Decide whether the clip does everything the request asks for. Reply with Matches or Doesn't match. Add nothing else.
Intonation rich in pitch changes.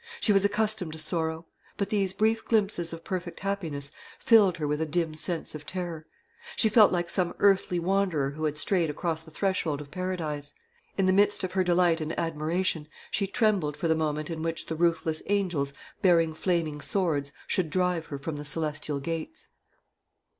Doesn't match